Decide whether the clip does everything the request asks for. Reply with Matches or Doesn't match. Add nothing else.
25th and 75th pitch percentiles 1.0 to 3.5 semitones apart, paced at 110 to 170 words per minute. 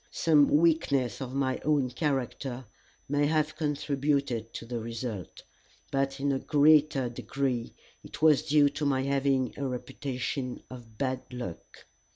Matches